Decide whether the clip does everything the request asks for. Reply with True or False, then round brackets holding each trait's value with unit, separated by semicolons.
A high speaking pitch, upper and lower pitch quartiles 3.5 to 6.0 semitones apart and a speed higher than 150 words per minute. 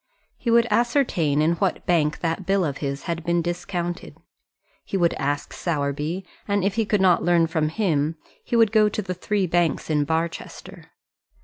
False (175 Hz; 3.9 semitones; 180 wpm)